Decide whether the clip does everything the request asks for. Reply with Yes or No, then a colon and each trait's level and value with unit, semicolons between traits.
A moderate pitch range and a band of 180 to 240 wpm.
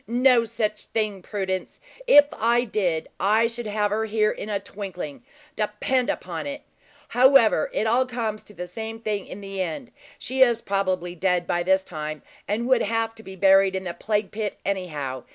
Yes: average, 3.3 semitones; average, 185 wpm